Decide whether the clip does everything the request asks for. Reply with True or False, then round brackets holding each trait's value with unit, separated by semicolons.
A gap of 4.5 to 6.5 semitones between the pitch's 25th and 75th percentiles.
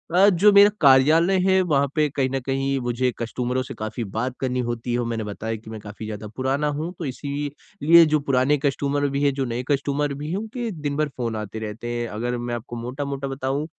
False (3.6 semitones)